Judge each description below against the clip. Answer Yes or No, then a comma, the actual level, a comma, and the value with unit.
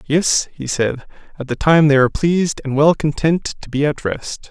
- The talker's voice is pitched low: No, medium, 150 Hz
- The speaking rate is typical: No, fast, 215 wpm